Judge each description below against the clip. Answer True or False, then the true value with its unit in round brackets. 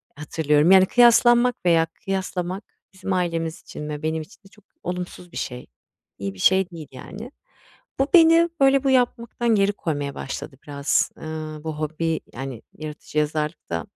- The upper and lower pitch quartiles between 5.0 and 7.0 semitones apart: True (5.3 semitones)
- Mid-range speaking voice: True (165 Hz)